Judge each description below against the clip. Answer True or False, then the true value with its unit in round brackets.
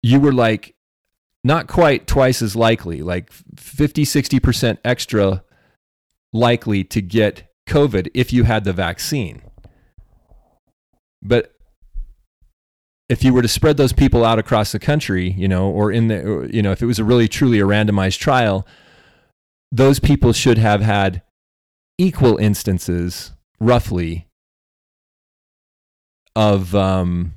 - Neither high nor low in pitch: False (105 Hz)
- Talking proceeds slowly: True (125 wpm)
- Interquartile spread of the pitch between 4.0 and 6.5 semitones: True (4.8 semitones)